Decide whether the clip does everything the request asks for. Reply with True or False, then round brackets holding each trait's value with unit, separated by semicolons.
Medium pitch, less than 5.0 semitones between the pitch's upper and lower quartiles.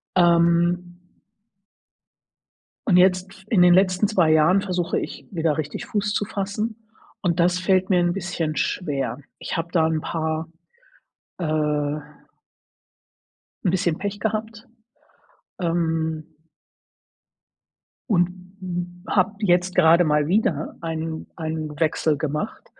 True (175 Hz; 2.8 semitones)